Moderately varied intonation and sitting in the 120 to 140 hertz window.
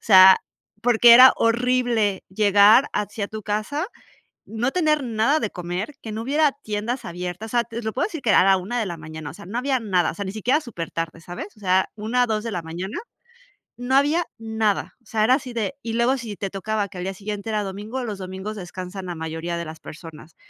No: average, 4.2 semitones; high, 215 Hz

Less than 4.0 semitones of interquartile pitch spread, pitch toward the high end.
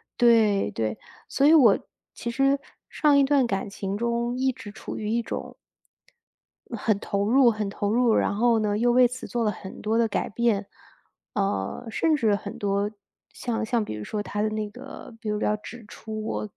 Yes: average, 2.9 semitones; high, 220 Hz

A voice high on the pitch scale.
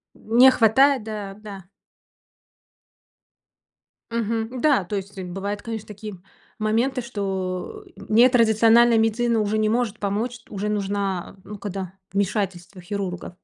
Yes: high, 215 Hz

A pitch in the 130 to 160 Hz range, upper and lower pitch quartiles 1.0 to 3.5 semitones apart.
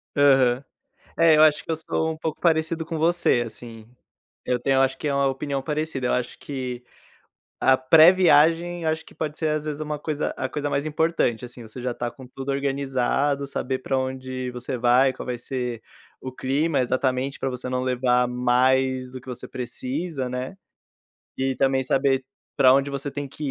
Yes: low, 135 Hz; average, 2.9 semitones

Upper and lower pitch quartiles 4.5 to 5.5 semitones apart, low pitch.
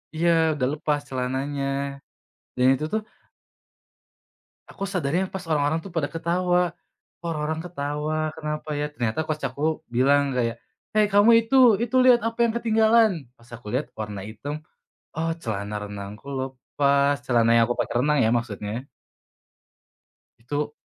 No: average, 5.1 semitones; medium, 145 Hz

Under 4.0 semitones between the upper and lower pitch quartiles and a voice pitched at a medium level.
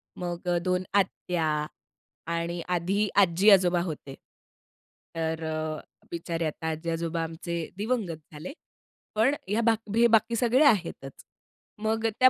No: average, 4.5 semitones; medium, 175 Hz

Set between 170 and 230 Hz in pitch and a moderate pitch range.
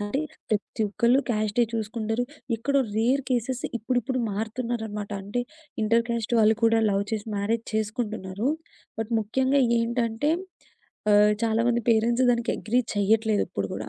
No: high, 225 Hz; narrow, 2.1 semitones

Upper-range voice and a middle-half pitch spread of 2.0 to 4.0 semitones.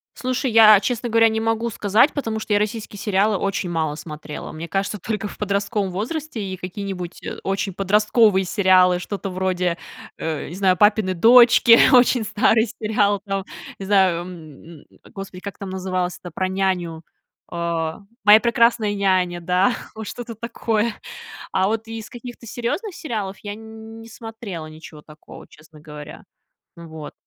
Yes: high, 200 Hz; average, 3.5 semitones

